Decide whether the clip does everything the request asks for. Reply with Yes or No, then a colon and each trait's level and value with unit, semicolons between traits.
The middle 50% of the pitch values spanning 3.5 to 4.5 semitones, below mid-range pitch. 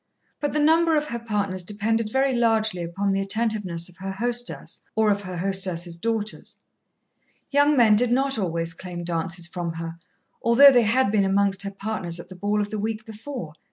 No: average, 4.2 semitones; high, 205 Hz